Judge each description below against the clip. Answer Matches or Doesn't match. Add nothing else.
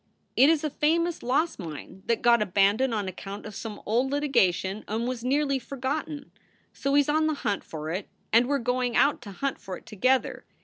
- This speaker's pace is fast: Matches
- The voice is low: Doesn't match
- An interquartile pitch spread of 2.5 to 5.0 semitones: Doesn't match